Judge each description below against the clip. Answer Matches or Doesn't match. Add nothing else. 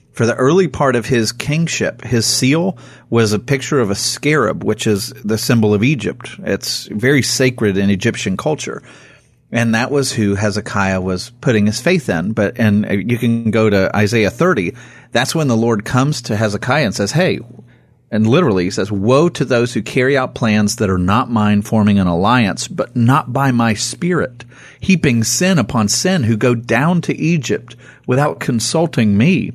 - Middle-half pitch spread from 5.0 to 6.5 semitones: Doesn't match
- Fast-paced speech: Doesn't match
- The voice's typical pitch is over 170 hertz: Doesn't match